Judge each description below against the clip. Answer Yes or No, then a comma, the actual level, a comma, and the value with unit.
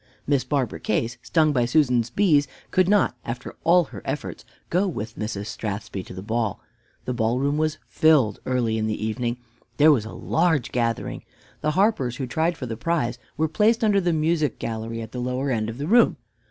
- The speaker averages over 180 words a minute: Yes, average, 195 wpm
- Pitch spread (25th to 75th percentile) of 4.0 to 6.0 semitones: Yes, wide, 5.6 semitones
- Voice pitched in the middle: No, low, 125 Hz